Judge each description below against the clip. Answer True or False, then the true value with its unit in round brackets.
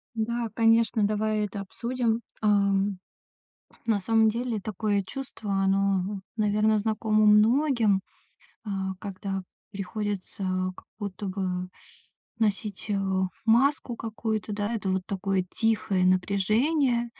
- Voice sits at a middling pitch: False (210 Hz)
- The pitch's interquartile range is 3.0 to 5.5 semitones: False (2.4 semitones)